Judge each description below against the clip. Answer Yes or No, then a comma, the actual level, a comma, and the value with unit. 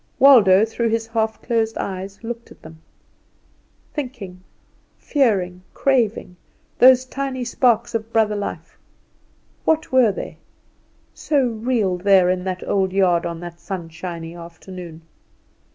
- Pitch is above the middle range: Yes, high, 210 Hz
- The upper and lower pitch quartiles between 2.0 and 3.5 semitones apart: No, average, 4.8 semitones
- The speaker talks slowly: Yes, slow, 120 wpm